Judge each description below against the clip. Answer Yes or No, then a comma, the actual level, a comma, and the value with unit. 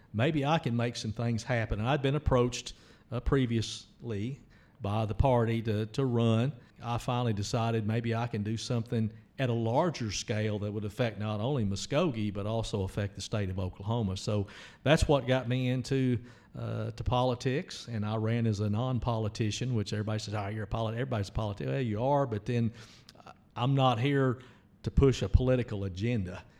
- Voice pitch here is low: Yes, low, 115 Hz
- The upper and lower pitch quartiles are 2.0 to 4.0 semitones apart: Yes, average, 2.7 semitones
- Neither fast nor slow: Yes, average, 185 wpm